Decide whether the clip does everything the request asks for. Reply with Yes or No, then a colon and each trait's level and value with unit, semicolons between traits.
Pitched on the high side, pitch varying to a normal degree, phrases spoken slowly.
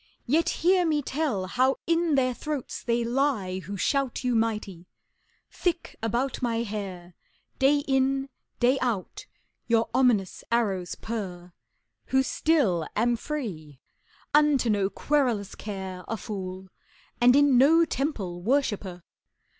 No: high, 235 Hz; wide, 6.0 semitones; slow, 125 wpm